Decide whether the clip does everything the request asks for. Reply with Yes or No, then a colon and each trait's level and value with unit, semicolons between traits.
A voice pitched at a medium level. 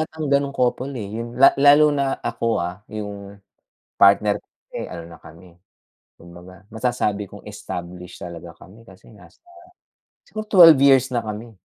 No: low, 105 Hz